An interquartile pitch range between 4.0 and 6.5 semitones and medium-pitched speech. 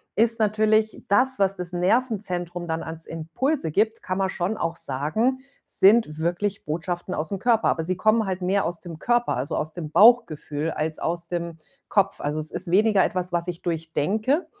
Yes: average, 4.8 semitones; medium, 180 Hz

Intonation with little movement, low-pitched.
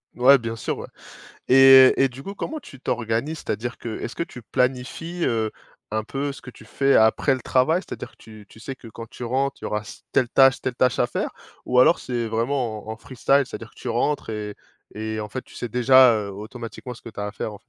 No: average, 3.1 semitones; low, 125 Hz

